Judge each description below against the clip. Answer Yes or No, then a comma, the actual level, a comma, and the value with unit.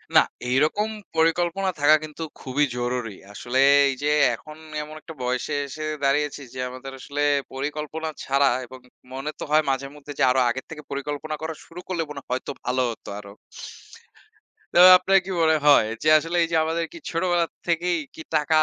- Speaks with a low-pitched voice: No, medium, 150 Hz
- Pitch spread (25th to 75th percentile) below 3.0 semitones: No, average, 3.4 semitones